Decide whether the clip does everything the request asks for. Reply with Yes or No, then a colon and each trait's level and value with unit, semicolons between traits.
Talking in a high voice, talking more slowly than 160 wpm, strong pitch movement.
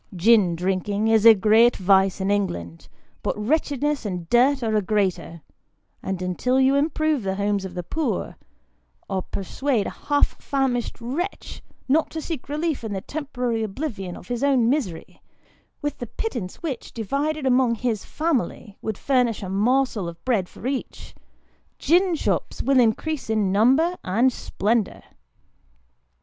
Yes: high, 230 Hz; average, 150 wpm; wide, 6.0 semitones